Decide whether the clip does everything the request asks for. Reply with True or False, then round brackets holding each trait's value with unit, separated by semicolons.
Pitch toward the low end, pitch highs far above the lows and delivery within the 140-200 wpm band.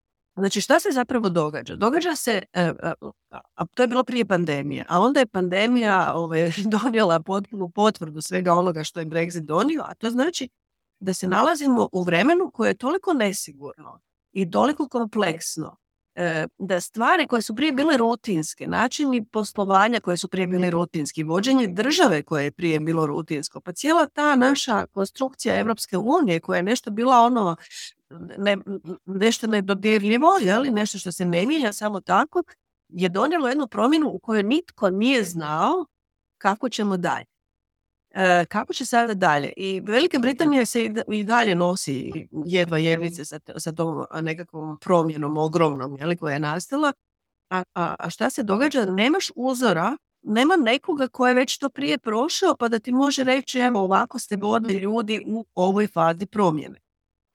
False (205 Hz; 6.4 semitones; 160 wpm)